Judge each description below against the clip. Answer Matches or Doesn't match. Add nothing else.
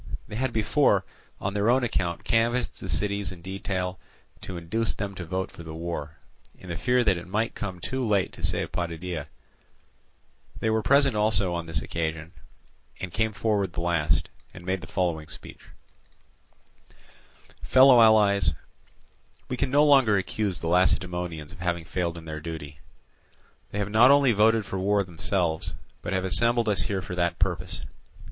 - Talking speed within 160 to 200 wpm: Matches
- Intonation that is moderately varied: Matches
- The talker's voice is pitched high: Doesn't match